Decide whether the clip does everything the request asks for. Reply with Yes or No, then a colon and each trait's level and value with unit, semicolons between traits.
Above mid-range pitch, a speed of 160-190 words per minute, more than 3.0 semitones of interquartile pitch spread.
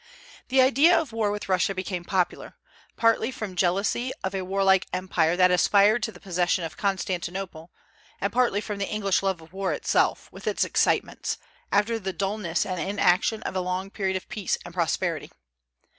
No: high, 195 Hz; average, 175 wpm; narrow, 2.6 semitones